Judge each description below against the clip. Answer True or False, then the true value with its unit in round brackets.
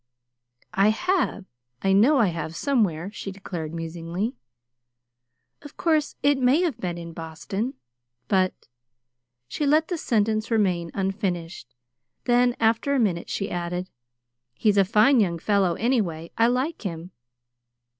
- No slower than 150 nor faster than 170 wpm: False (135 wpm)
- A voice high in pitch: True (200 Hz)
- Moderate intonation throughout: False (6.2 semitones)